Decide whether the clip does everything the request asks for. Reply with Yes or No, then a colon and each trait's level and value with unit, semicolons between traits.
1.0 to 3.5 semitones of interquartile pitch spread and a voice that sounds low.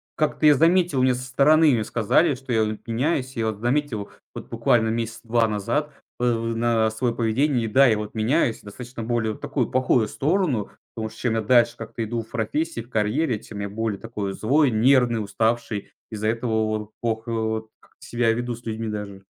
Yes: average, 2.7 semitones; low, 115 Hz